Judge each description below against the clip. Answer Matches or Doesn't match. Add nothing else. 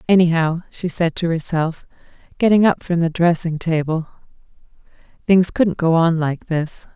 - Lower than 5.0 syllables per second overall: Matches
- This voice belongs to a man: Doesn't match